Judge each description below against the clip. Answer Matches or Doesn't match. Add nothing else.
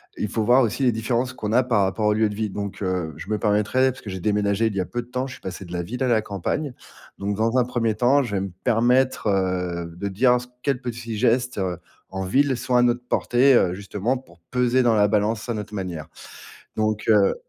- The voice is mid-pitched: Doesn't match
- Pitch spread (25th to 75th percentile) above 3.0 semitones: Matches